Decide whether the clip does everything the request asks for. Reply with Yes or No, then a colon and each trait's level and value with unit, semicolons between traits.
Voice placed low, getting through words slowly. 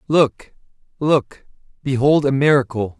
Yes: low, 130 Hz; slow, 100 wpm